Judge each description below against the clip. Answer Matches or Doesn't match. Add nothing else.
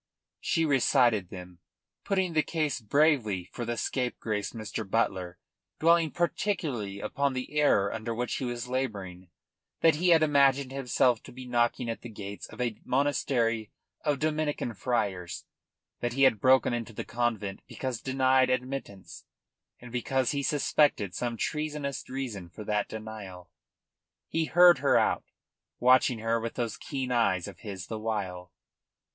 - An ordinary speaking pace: Matches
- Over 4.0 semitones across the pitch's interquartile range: Matches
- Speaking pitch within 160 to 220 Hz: Doesn't match